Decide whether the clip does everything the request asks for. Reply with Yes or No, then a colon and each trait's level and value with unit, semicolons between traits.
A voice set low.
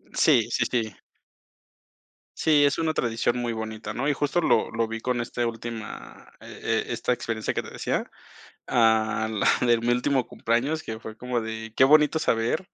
Yes: low, 115 Hz